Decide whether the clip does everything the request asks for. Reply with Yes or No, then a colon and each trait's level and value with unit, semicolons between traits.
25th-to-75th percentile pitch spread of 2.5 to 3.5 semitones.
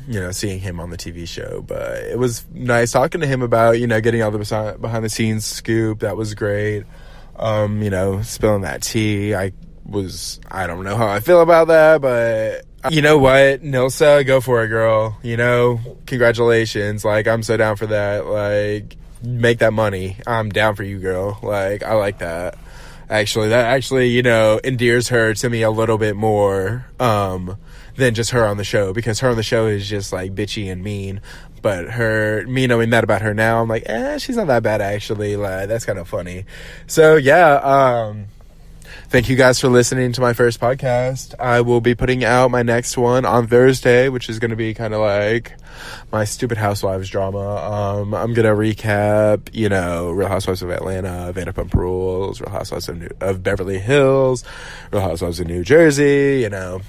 Yes: average, 3.2 semitones